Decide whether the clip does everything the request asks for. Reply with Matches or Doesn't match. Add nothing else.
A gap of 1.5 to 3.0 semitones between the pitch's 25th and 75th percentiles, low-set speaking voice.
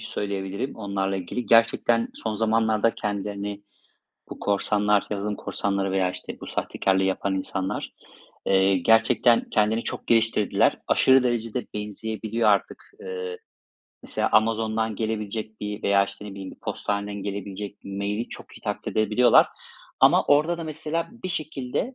Matches